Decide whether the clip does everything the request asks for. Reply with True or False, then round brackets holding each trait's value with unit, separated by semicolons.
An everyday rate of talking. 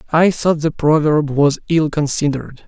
True (155 wpm)